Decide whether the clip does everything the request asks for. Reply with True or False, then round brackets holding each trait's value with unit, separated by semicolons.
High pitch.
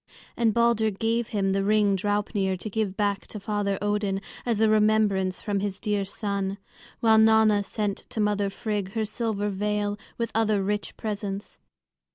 True (205 Hz)